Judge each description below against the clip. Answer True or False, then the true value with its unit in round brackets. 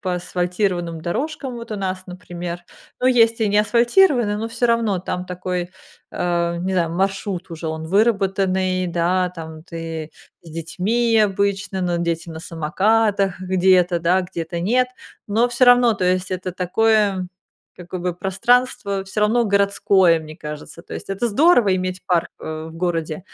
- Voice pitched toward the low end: False (185 Hz)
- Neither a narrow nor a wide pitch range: True (3.4 semitones)